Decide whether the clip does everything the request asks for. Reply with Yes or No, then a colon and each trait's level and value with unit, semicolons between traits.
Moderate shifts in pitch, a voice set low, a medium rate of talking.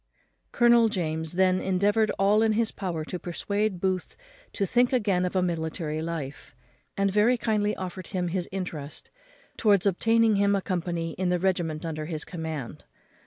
No: average, 3.7 semitones; medium, 185 Hz; average, 165 wpm